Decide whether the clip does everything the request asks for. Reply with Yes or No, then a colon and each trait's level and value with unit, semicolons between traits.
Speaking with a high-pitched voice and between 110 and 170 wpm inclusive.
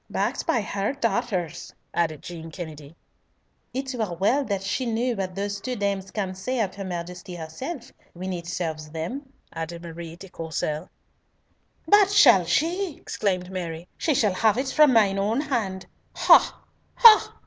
Yes: high, 195 Hz; average, 160 wpm